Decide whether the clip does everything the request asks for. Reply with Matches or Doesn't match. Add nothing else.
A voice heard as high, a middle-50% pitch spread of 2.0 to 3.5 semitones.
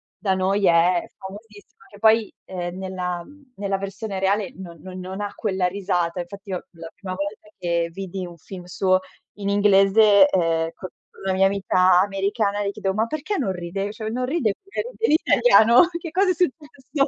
Matches